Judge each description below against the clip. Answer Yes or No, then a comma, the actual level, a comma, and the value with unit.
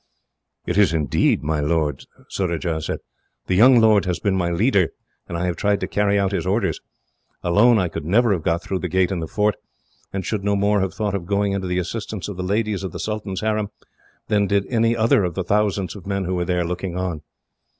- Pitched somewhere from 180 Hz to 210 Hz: No, very low, 95 Hz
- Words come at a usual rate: No, fast, 225 wpm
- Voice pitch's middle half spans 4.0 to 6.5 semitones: No, average, 2.8 semitones